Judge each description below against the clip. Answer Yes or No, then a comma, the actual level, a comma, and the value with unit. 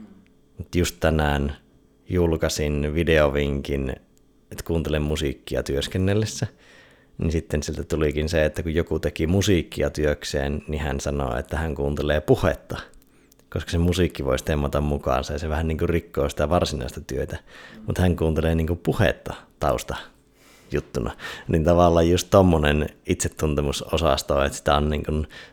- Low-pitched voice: Yes, very low, 75 Hz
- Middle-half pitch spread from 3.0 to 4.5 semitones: No, narrow, 2.6 semitones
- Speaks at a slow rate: No, average, 135 wpm